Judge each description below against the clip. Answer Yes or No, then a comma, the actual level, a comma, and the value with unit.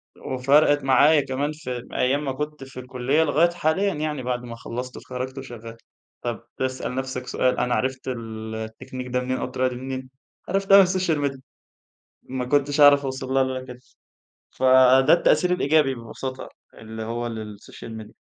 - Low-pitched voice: Yes, low, 130 Hz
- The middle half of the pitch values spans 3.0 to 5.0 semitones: No, narrow, 2.5 semitones